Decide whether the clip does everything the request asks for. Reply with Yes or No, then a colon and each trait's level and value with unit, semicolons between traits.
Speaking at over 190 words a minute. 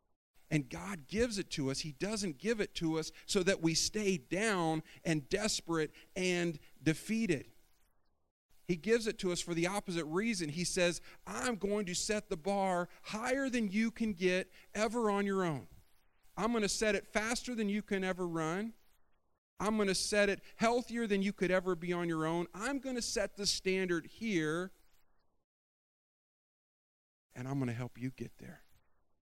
No: average, 180 wpm